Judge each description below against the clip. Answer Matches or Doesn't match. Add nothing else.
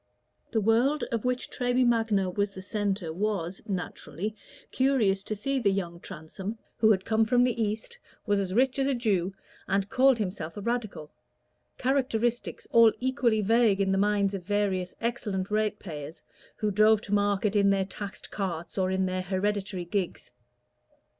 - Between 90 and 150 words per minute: Doesn't match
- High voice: Matches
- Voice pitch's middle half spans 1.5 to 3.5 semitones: Matches